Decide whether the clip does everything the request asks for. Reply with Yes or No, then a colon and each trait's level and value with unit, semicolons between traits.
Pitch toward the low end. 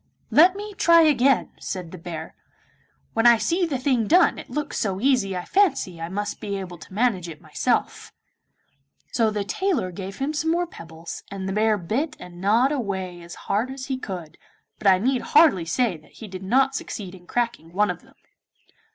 No: high, 210 Hz